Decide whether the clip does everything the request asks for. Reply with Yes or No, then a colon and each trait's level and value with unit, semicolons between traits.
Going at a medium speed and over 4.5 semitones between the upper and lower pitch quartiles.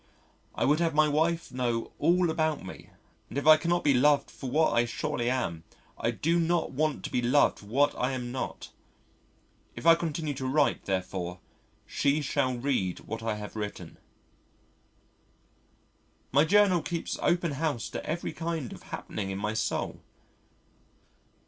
Yes: average, 160 wpm; average, 5.1 semitones